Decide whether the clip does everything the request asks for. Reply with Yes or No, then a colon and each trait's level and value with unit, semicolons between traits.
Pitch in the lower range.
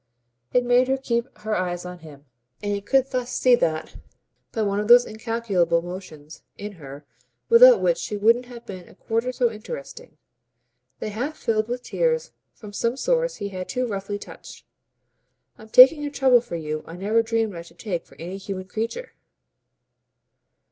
No: high, 220 Hz